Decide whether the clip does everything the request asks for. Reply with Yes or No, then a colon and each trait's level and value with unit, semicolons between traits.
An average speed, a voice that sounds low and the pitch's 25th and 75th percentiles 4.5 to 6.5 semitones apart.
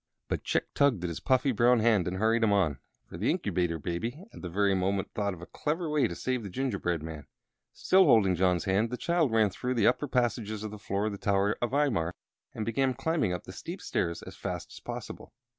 No: fast, 230 wpm; low, 105 Hz; average, 5.2 semitones